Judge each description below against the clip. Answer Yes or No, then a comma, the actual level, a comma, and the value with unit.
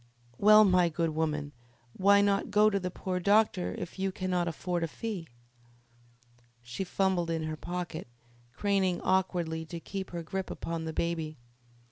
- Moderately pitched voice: Yes, medium, 180 Hz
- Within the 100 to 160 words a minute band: Yes, average, 155 wpm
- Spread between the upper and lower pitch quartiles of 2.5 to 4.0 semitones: Yes, average, 2.8 semitones